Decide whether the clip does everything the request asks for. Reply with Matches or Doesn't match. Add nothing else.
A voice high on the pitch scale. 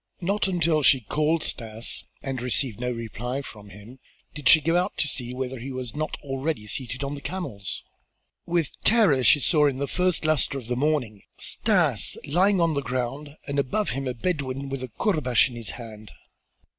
Doesn't match